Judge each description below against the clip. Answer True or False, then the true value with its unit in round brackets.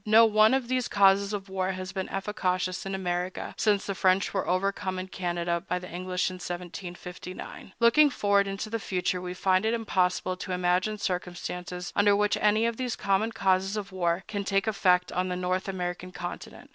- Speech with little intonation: True (2.1 semitones)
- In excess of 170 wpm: True (190 wpm)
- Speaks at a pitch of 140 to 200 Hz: True (190 Hz)